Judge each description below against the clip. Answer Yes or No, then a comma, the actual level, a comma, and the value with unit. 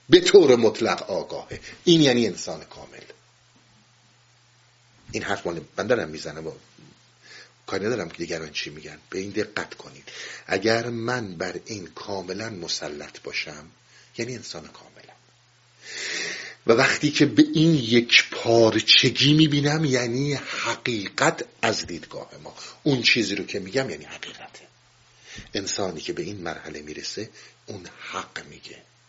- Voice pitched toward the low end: Yes, low, 120 Hz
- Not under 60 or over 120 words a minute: No, average, 130 wpm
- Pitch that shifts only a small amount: No, average, 4.8 semitones